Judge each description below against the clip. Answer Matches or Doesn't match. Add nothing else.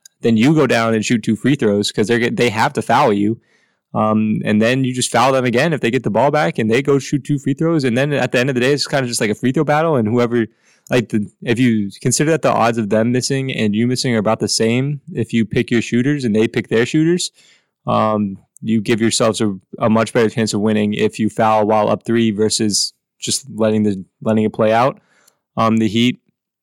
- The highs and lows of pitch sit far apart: Doesn't match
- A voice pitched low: Matches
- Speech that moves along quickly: Matches